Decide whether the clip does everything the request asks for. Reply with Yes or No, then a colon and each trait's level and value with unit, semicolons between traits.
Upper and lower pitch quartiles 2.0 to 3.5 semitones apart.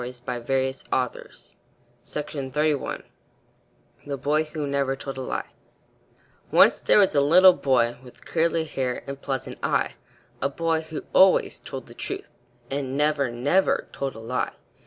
Yes: average, 2.8 semitones